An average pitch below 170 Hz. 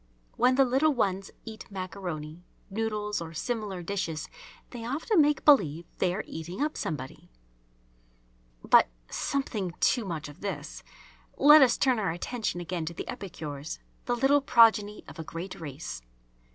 No: high, 200 Hz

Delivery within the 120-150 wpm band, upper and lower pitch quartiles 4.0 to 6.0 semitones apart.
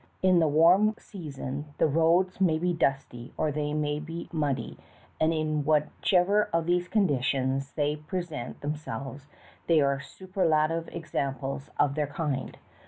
No: average, 140 wpm; average, 3.2 semitones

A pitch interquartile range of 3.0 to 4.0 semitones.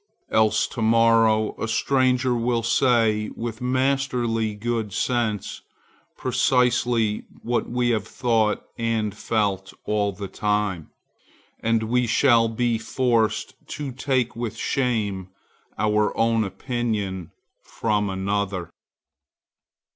No: narrow, 2.4 semitones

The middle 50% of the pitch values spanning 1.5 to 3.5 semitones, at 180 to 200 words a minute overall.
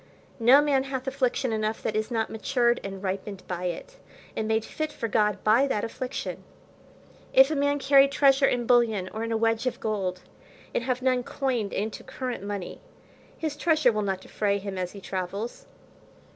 No: average, 4.5 semitones; average, 185 wpm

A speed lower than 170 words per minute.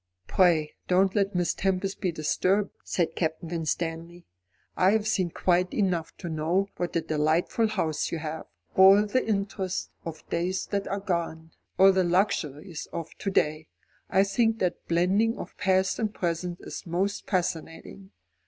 Yes: average, 155 wpm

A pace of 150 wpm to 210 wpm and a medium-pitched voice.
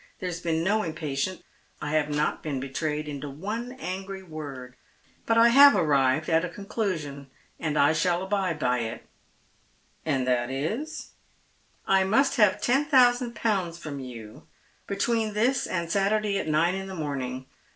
Yes: average, 170 wpm; medium, 170 Hz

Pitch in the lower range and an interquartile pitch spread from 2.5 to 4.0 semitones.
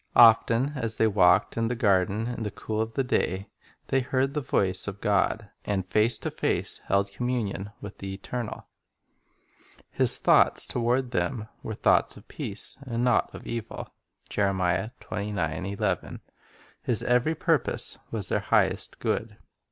Yes: low, 110 Hz; average, 3.7 semitones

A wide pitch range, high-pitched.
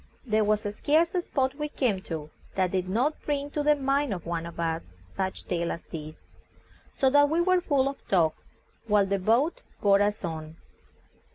Yes: wide, 8.5 semitones; high, 210 Hz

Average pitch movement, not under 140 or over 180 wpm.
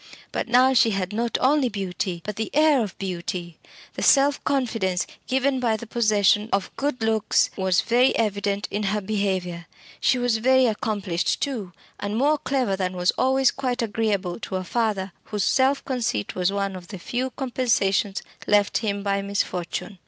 Yes: average, 4.4 semitones; average, 170 wpm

